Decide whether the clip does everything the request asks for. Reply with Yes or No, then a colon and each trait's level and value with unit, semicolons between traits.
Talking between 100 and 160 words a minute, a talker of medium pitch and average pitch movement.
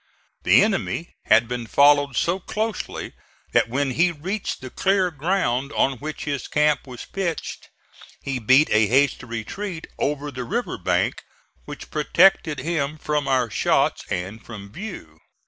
No: average, 145 wpm; medium, 145 Hz; wide, 5.7 semitones